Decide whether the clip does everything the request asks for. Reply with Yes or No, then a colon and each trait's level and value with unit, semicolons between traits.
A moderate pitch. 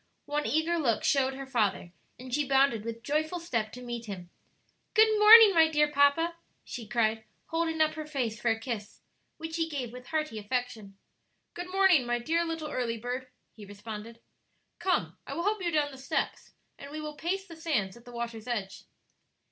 No: very high, 270 Hz